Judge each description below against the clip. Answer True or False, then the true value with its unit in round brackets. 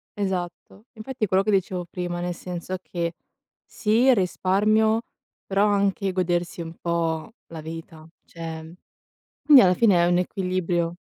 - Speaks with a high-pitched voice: False (180 Hz)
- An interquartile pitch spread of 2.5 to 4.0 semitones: True (2.8 semitones)